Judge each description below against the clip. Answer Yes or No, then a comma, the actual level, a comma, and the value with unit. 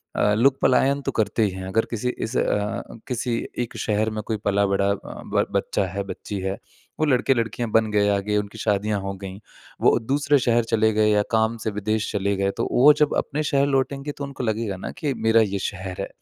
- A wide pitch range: No, average, 3.7 semitones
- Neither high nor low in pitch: No, low, 110 Hz